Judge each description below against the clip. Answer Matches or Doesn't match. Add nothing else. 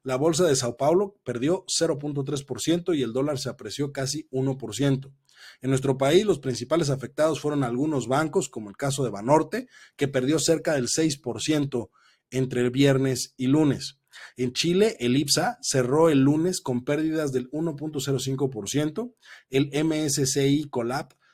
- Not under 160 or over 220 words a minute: Doesn't match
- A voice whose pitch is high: Doesn't match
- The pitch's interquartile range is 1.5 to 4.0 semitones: Matches